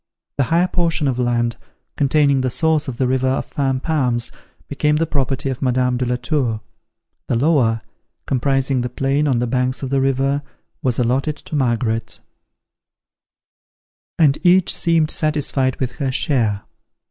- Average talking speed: Yes, average, 155 wpm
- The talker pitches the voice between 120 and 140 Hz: Yes, low, 135 Hz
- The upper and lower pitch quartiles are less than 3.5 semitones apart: Yes, average, 2.9 semitones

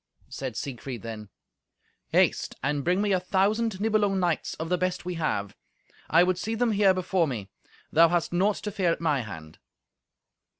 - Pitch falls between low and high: Yes, medium, 175 Hz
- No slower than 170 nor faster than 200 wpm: Yes, average, 175 wpm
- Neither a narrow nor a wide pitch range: No, wide, 5.9 semitones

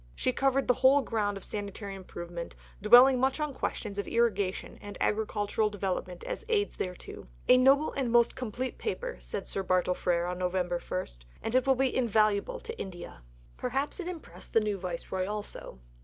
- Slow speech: No, average, 175 wpm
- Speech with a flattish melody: No, wide, 5.5 semitones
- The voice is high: Yes, high, 215 Hz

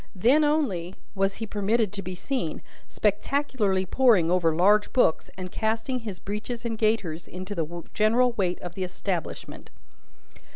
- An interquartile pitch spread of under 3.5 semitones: No, average, 4.0 semitones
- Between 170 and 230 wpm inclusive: No, average, 150 wpm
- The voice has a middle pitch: No, high, 205 Hz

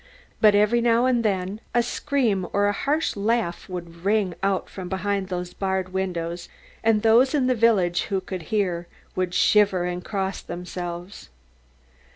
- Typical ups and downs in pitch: Yes, average, 3.5 semitones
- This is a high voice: Yes, high, 195 Hz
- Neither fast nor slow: Yes, average, 160 wpm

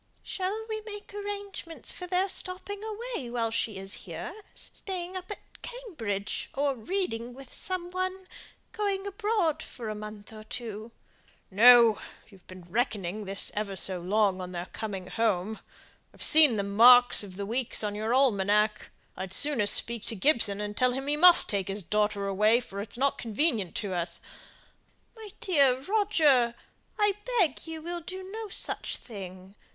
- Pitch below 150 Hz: No, high, 240 Hz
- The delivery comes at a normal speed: Yes, average, 165 wpm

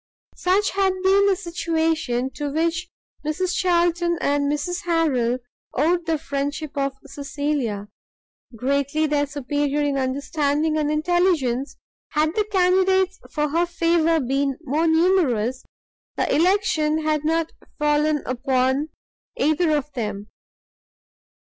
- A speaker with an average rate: No, slow, 115 wpm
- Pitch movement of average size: Yes, average, 3.5 semitones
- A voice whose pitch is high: Yes, very high, 305 Hz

